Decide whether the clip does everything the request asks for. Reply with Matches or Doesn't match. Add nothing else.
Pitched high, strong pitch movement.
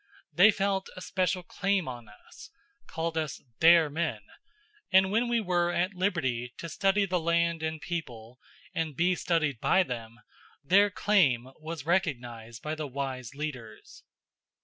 Doesn't match